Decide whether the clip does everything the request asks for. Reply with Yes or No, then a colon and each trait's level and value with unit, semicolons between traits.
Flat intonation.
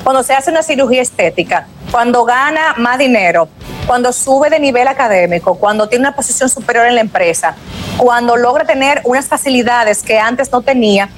No: average, 3.2 semitones